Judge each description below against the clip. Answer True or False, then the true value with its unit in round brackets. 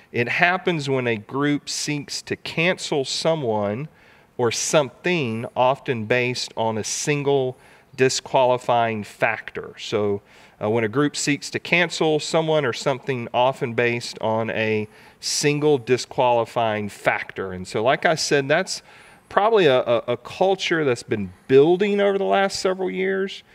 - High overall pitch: False (135 Hz)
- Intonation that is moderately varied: False (5.7 semitones)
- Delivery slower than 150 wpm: True (140 wpm)